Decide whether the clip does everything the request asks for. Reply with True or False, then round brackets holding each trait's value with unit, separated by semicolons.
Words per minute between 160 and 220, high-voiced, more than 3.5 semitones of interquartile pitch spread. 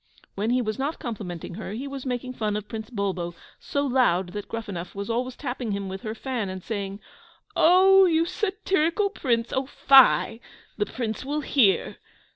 True (175 wpm; 235 Hz; 5.2 semitones)